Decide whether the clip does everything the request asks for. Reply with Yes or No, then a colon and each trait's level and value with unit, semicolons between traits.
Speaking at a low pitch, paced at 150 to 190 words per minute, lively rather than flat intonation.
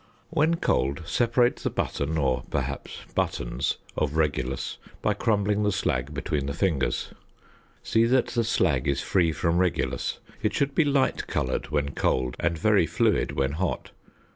Yes: very low, 80 Hz; average, 155 wpm; wide, 8.0 semitones